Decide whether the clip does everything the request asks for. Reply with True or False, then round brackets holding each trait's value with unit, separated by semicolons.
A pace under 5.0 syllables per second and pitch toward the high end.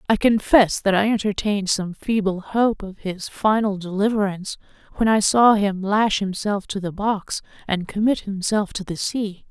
True (4.6 syllables/s; 205 Hz)